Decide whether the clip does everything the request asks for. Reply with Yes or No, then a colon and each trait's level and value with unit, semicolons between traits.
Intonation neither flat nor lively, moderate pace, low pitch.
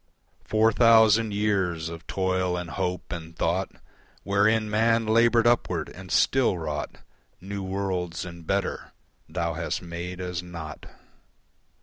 No: average, 3.9 semitones; slow, 125 wpm; very low, 95 Hz